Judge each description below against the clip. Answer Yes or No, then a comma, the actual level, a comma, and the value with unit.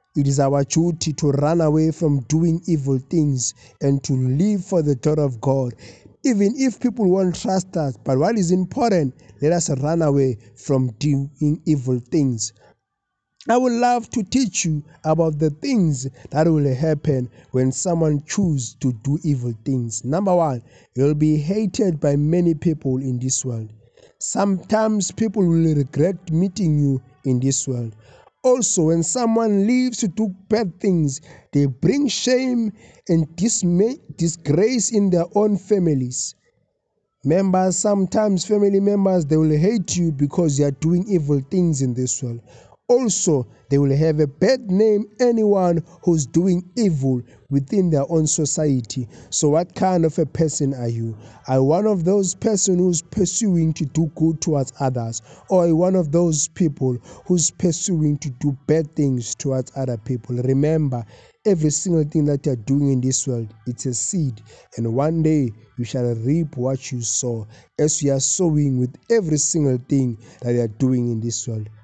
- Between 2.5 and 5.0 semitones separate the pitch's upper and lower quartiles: No, wide, 5.6 semitones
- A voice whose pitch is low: No, medium, 155 Hz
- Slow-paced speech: No, average, 165 wpm